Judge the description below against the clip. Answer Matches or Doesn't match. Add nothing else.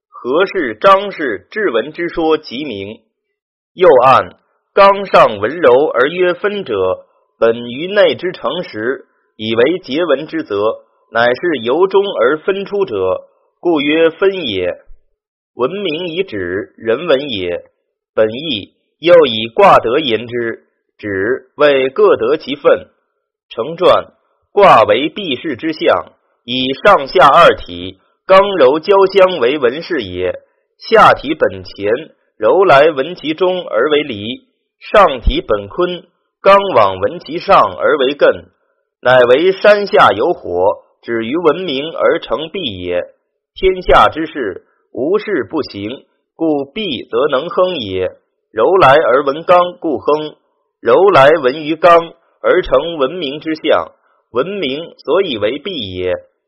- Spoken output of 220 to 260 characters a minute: Doesn't match